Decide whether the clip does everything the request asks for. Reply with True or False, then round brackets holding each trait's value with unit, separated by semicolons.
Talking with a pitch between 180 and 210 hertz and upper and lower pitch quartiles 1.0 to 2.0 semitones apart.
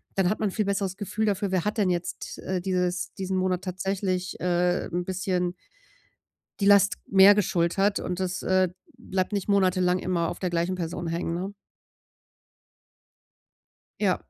True (185 Hz; 1.7 semitones)